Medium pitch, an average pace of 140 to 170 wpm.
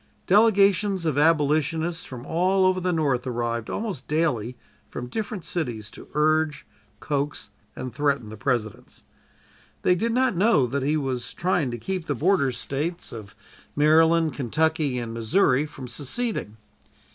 Yes: medium, 150 Hz; average, 145 wpm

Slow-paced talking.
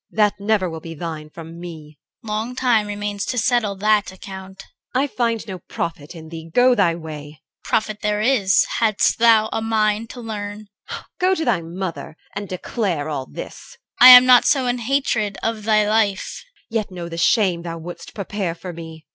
No: average, 200 wpm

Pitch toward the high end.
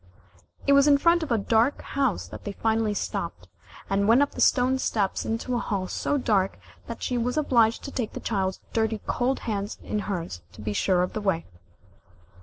Yes: high, 225 Hz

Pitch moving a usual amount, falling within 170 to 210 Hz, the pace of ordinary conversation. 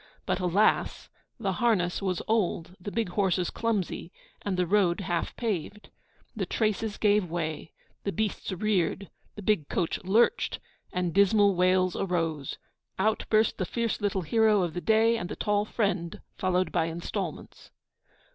Yes: average, 3.2 semitones; high, 190 Hz; average, 150 wpm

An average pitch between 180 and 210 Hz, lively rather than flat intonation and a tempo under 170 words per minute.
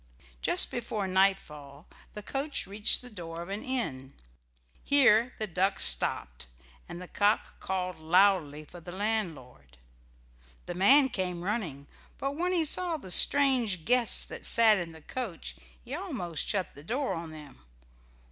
Yes: high, 190 Hz; wide, 6.2 semitones; average, 150 wpm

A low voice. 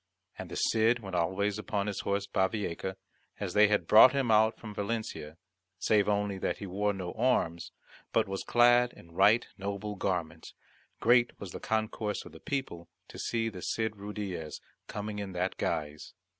Yes: low, 100 Hz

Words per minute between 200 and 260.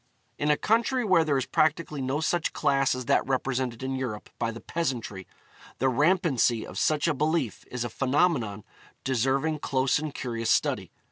No: average, 175 wpm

